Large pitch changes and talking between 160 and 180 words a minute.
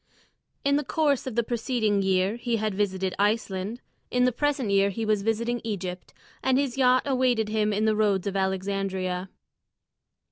No: average, 3.8 semitones; average, 170 wpm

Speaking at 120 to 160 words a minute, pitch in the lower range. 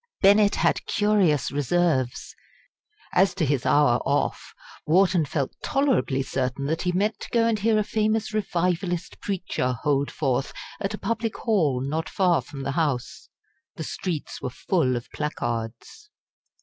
No: average, 150 wpm; medium, 160 Hz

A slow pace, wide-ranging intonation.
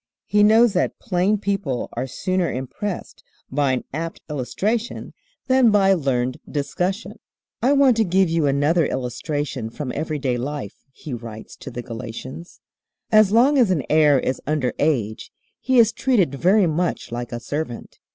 No: average, 155 wpm; wide, 7.6 semitones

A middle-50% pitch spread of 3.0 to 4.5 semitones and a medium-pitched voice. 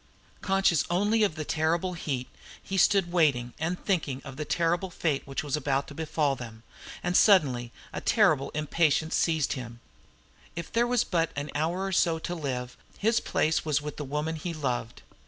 Yes: average, 4.1 semitones; medium, 155 Hz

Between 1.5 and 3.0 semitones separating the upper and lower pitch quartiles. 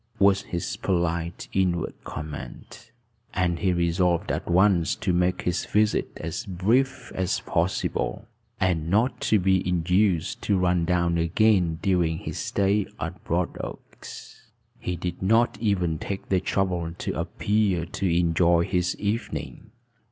Yes: narrow, 2.6 semitones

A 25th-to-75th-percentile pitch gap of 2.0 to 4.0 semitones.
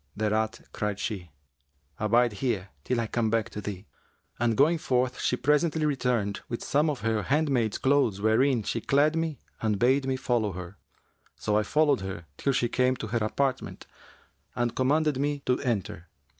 No: average, 4.4 semitones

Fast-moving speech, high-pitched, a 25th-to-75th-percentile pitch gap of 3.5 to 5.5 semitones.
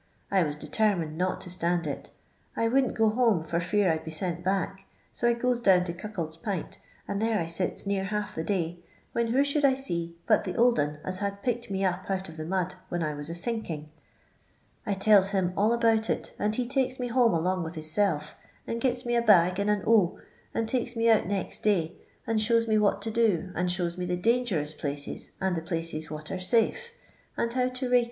Yes: fast, 225 wpm; high, 195 Hz; average, 5.0 semitones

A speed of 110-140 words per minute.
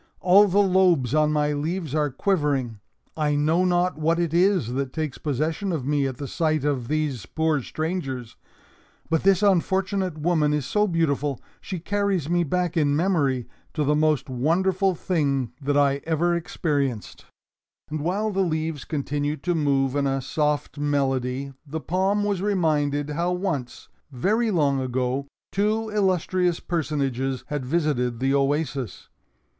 No: average, 150 wpm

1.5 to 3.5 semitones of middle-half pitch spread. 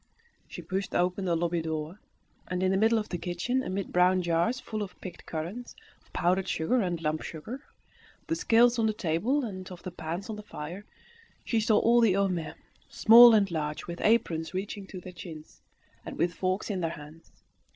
No: average, 4.2 semitones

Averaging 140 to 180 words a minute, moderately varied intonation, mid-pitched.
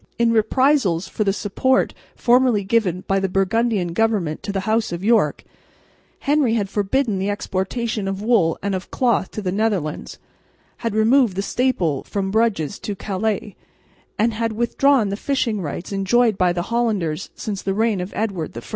No: average, 170 wpm; average, 3.3 semitones; high, 205 Hz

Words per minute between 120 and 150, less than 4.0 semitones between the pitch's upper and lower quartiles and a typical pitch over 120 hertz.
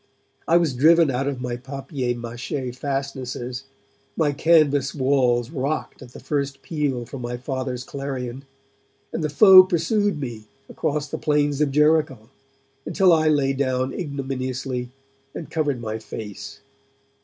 Yes: average, 140 wpm; average, 3.1 semitones; low, 135 Hz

